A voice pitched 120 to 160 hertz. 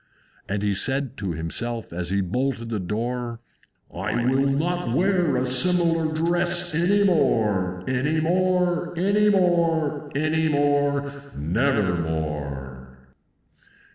Yes: medium, 140 Hz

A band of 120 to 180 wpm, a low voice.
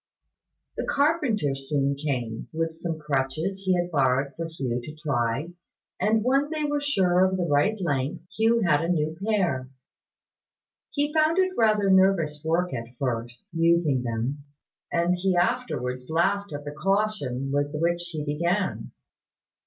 No: average, 150 wpm; medium, 165 Hz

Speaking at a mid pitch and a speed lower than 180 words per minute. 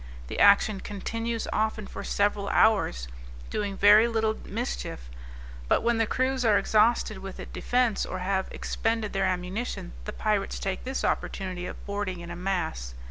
No: high, 205 Hz; average, 160 wpm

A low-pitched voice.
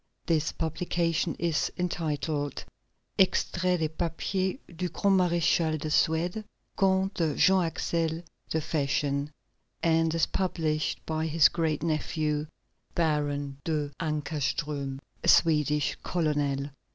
No: medium, 160 Hz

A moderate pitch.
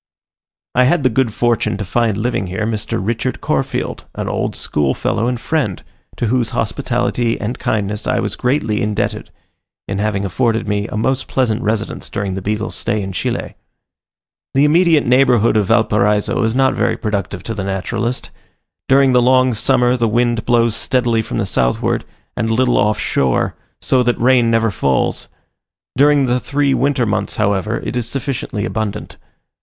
No: low, 115 Hz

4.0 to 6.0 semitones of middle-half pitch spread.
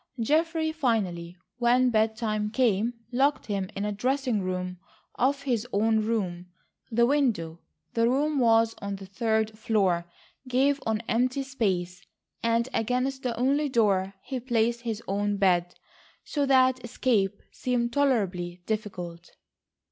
Yes: average, 4.5 semitones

